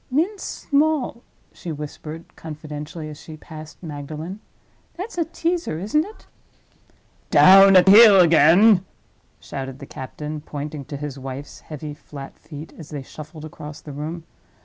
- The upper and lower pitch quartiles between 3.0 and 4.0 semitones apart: No, average, 4.8 semitones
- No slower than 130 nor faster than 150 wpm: Yes, average, 140 wpm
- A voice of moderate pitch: Yes, medium, 155 Hz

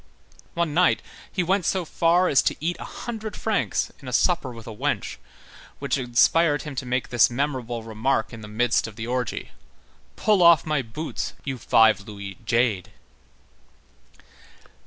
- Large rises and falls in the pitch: Yes, wide, 6.6 semitones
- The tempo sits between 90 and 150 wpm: No, average, 160 wpm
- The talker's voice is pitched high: No, low, 130 Hz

